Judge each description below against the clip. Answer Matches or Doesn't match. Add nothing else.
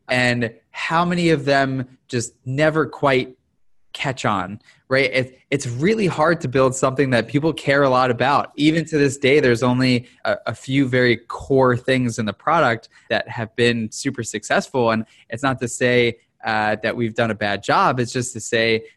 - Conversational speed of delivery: Matches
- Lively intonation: Doesn't match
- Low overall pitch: Matches